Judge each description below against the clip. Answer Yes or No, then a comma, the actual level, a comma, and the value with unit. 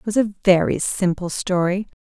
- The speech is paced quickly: No, average, 175 wpm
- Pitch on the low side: No, high, 190 Hz